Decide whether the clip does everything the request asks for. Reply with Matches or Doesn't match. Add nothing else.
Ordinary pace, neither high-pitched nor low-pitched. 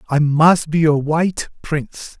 Matches